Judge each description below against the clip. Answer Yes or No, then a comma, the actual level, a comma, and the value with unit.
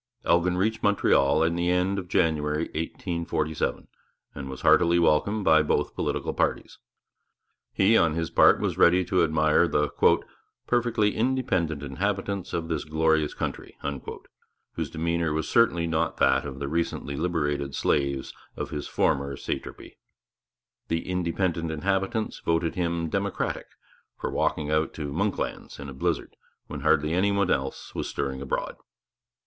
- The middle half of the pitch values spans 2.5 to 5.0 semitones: Yes, average, 3.4 semitones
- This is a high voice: No, very low, 80 Hz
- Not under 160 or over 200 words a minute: No, average, 145 wpm